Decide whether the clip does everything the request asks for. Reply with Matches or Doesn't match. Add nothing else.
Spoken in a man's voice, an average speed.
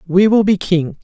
Doesn't match